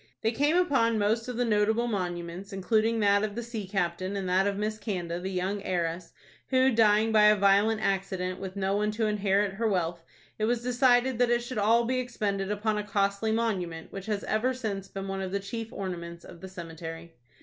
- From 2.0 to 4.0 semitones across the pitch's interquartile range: Yes, average, 3.0 semitones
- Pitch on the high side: Yes, high, 205 Hz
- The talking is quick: Yes, fast, 210 wpm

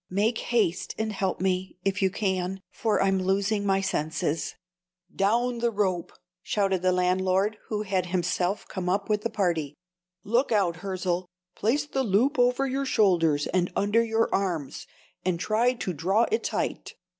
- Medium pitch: No, high, 195 Hz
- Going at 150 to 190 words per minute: Yes, average, 165 wpm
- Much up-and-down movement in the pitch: No, average, 3.3 semitones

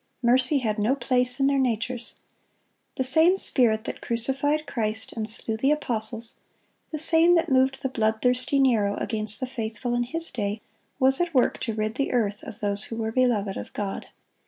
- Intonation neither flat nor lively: Yes, average, 3.6 semitones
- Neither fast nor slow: Yes, average, 180 wpm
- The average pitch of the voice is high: Yes, high, 245 Hz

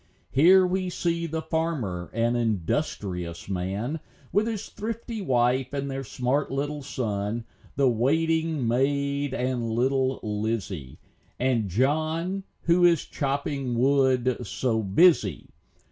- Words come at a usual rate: No, slow, 115 wpm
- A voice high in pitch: No, low, 135 Hz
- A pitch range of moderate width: No, wide, 5.7 semitones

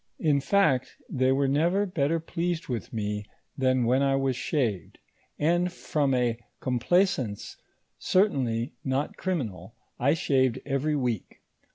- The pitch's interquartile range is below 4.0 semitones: No, average, 4.6 semitones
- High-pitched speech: No, low, 135 Hz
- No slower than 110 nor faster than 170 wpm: Yes, slow, 135 wpm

